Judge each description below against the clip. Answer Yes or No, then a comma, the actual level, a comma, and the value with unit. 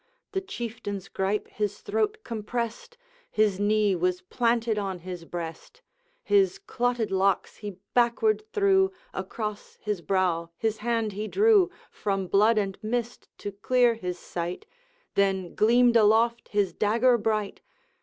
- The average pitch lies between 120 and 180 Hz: No, high, 215 Hz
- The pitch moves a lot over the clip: No, average, 3.7 semitones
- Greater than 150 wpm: No, slow, 135 wpm